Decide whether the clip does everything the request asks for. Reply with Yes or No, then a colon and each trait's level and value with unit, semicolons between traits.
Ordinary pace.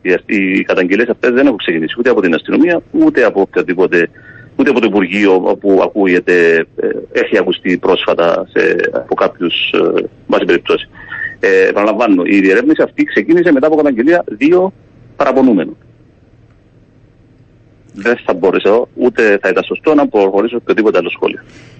Yes: average, 130 wpm